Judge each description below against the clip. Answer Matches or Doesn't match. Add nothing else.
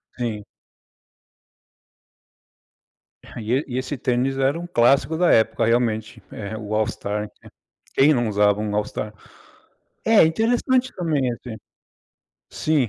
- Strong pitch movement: Matches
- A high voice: Doesn't match